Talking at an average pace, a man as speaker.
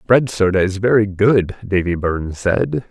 Yes: average, 145 wpm; male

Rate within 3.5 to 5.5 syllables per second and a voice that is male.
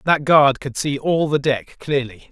Yes: 4.2 syllables/s; male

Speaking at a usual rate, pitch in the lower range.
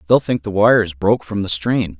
No: fast, 240 wpm; low, 100 Hz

